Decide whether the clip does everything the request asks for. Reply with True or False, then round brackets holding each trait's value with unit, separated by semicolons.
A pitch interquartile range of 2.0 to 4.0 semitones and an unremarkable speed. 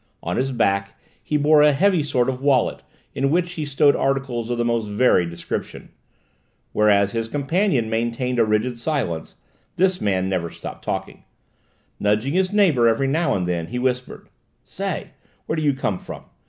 False (5.4 semitones; 170 wpm)